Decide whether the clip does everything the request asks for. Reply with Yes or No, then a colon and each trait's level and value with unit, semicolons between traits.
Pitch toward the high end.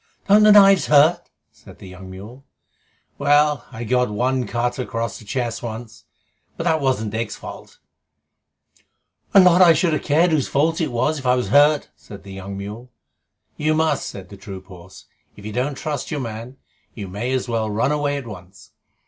No: low, 125 Hz